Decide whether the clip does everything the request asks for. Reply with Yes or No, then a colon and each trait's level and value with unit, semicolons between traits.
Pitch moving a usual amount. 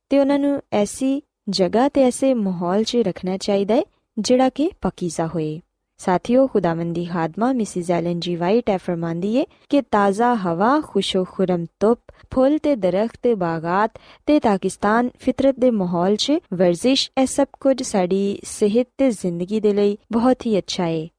No: wide, 6.0 semitones